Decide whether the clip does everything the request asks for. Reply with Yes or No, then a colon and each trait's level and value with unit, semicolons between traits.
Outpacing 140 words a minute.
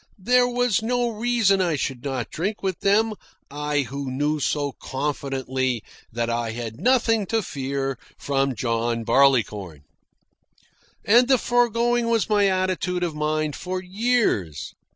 No: slow, 135 wpm